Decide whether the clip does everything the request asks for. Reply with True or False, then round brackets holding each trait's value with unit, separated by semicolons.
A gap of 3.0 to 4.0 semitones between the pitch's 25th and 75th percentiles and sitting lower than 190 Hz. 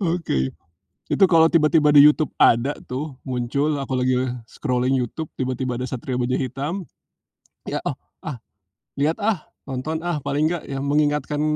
True (3.3 semitones; 140 Hz)